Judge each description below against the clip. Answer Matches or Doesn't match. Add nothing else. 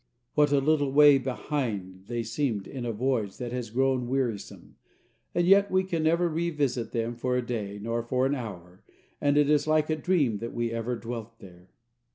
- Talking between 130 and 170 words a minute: Doesn't match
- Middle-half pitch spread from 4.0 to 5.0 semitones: Matches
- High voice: Doesn't match